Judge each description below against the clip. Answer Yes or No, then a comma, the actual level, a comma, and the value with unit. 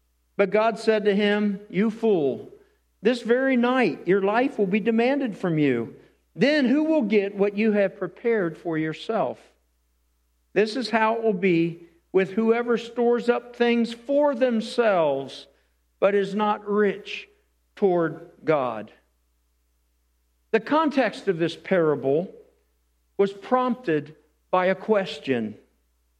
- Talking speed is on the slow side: Yes, slow, 130 wpm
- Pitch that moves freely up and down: Yes, wide, 7.2 semitones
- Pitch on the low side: No, high, 200 Hz